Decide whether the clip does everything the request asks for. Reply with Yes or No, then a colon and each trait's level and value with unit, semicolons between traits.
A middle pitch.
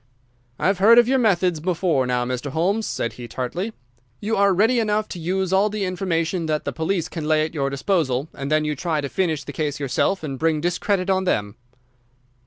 Yes: medium, 170 Hz